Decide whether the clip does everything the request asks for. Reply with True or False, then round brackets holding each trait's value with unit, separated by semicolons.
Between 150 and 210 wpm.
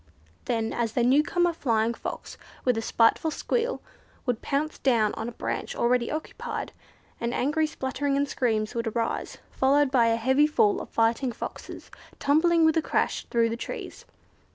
True (165 wpm)